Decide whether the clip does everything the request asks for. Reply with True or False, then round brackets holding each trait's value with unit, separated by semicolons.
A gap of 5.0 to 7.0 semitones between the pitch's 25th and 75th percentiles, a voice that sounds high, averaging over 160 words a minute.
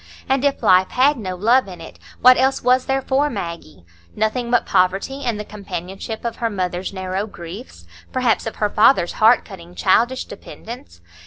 True (5.3 semitones; 215 Hz; 175 wpm)